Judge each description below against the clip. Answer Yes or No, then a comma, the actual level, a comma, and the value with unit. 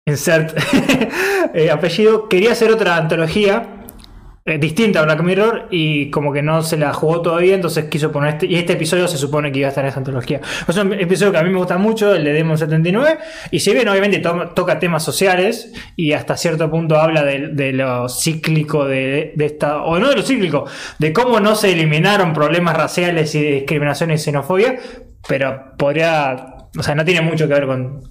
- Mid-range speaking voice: Yes, medium, 165 Hz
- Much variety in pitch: No, average, 4.6 semitones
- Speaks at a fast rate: Yes, fast, 205 wpm